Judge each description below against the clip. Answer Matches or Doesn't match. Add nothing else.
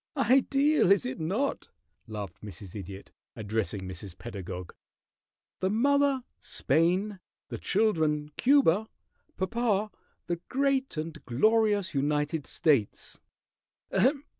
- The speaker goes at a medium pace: Doesn't match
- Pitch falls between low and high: Matches